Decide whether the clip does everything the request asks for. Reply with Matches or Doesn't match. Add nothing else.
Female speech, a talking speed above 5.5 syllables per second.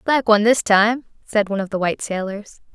Matches